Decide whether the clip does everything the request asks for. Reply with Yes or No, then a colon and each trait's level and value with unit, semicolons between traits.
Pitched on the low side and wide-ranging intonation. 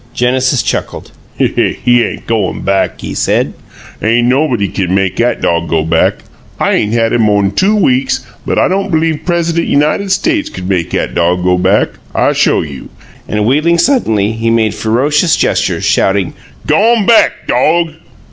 Yes: low, 120 Hz; wide, 8.4 semitones